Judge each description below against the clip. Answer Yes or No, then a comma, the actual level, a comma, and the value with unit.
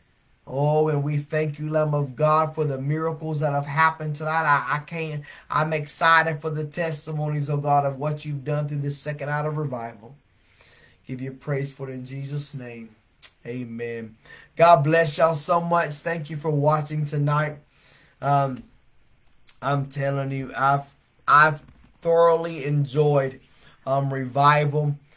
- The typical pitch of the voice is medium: Yes, medium, 145 Hz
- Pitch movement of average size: No, narrow, 2.2 semitones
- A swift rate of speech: No, average, 155 wpm